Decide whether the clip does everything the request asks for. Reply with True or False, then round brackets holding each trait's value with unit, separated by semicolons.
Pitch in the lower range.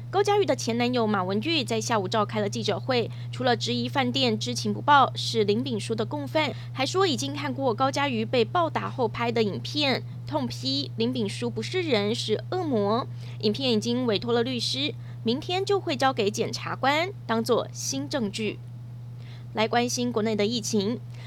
True (130 Hz)